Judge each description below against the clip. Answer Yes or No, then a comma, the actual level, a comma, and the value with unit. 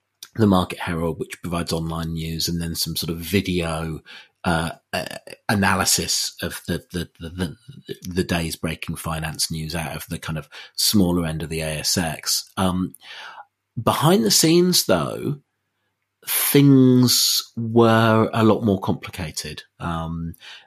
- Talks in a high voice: No, very low, 90 Hz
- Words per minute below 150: Yes, slow, 135 wpm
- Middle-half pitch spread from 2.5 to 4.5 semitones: No, average, 5.2 semitones